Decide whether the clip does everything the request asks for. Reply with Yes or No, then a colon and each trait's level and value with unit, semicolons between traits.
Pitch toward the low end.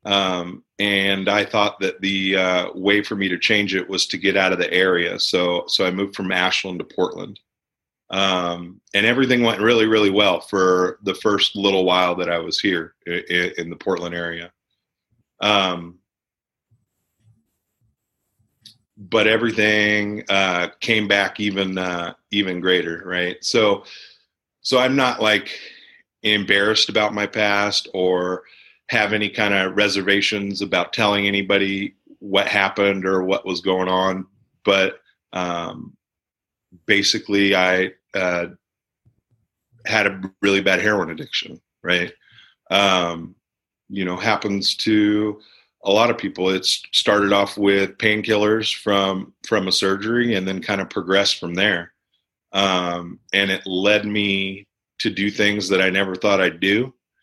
Yes: low, 100 Hz